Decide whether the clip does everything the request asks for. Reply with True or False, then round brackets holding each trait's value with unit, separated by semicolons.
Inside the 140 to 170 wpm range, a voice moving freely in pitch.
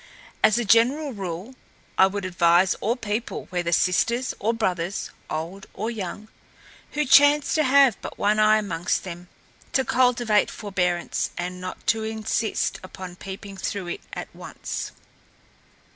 False (145 wpm; 4.3 semitones)